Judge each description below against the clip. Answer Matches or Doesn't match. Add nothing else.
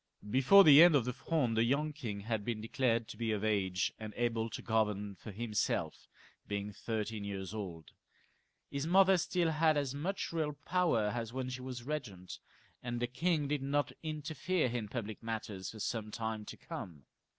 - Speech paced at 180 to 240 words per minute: Matches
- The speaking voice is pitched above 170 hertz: Doesn't match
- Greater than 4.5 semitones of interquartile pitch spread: Matches